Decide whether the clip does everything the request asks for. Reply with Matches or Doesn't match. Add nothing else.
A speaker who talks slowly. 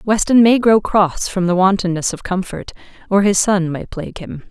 Doesn't match